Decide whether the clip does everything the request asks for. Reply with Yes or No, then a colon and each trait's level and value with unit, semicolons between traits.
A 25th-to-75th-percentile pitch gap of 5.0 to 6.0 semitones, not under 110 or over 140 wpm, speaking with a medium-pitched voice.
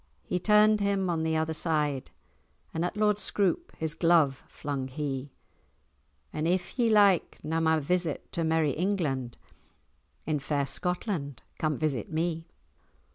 No: average, 3.8 semitones; slow, 135 wpm; medium, 160 Hz